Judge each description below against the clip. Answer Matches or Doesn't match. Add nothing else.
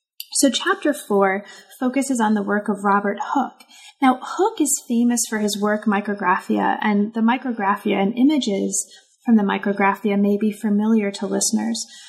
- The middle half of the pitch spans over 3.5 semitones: Matches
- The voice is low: Doesn't match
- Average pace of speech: Matches